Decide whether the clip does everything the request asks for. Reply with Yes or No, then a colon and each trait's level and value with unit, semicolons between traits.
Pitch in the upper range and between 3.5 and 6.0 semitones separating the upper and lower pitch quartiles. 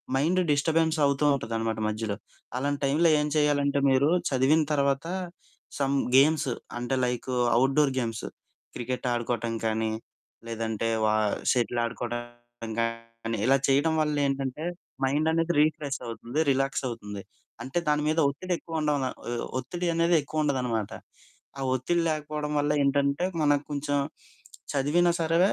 No: medium, 140 Hz; average, 3.9 semitones